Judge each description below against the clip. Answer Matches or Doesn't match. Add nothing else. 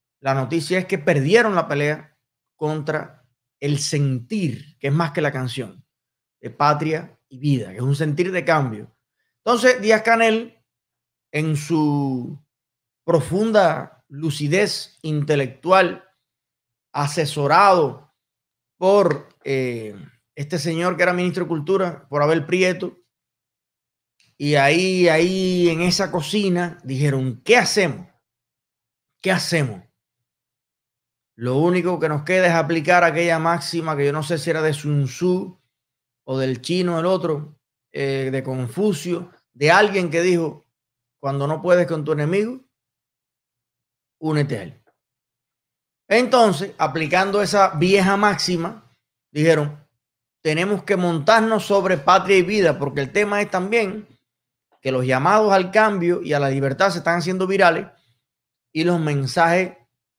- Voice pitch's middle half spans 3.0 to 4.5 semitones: Doesn't match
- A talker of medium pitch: Matches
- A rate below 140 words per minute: Matches